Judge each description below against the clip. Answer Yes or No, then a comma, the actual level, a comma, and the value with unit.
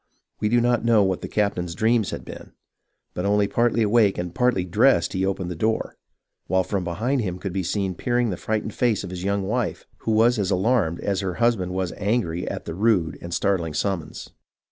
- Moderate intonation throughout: Yes, average, 3.8 semitones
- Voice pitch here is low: Yes, low, 100 Hz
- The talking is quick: Yes, fast, 210 wpm